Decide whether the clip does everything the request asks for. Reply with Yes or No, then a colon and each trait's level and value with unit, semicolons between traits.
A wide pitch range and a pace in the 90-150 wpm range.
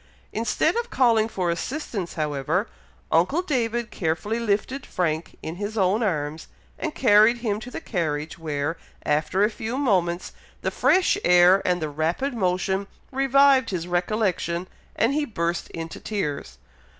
Yes: wide, 5.7 semitones; average, 145 wpm